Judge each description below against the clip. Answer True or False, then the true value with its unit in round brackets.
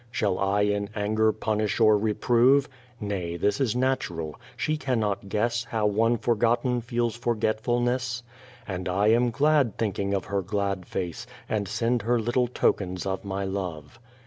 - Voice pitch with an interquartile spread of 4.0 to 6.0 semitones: False (3.3 semitones)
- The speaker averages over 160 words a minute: False (150 wpm)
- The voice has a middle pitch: False (110 Hz)